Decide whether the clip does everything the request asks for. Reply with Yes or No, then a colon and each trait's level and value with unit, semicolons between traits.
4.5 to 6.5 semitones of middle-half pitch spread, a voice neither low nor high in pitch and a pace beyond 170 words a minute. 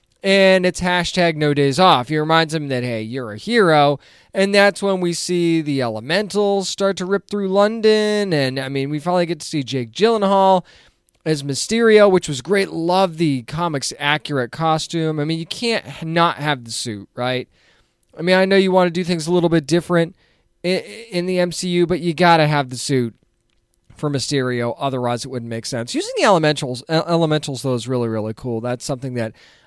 Yes: wide, 5.4 semitones; medium, 165 Hz; average, 200 wpm